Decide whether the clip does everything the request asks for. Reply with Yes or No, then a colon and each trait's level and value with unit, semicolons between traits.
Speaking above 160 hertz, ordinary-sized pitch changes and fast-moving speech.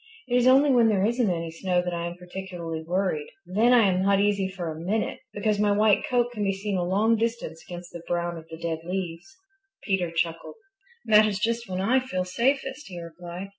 Yes: high, 190 Hz; average, 4.1 semitones; fast, 215 wpm